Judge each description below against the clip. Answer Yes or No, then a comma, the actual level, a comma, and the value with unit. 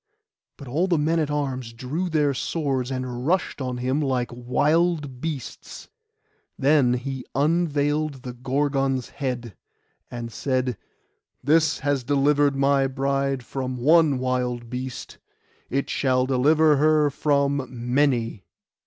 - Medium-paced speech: No, slow, 125 wpm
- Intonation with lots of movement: No, narrow, 2.6 semitones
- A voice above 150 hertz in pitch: No, low, 135 Hz